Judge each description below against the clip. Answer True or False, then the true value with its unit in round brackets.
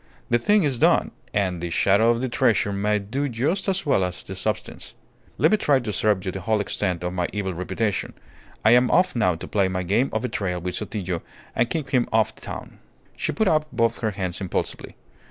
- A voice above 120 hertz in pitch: False (105 Hz)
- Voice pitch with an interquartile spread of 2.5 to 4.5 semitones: False (4.9 semitones)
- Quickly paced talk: True (225 wpm)